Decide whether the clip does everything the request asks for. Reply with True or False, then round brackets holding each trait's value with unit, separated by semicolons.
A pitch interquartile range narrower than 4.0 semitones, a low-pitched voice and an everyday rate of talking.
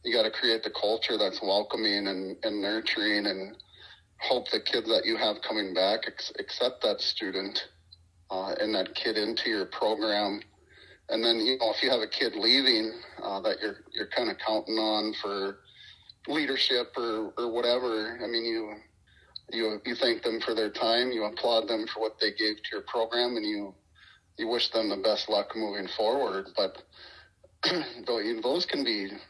True (2.4 semitones; 110 Hz; 180 wpm)